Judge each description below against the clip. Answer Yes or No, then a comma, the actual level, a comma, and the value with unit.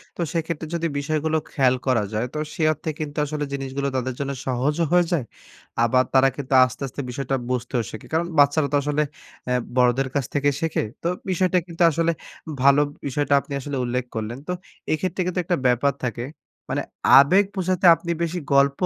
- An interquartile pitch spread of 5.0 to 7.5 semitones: No, average, 4.0 semitones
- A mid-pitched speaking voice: Yes, medium, 145 Hz